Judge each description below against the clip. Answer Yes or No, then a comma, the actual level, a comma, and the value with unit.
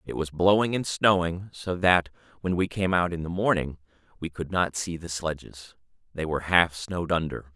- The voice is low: Yes, very low, 85 Hz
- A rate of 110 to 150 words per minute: No, average, 200 wpm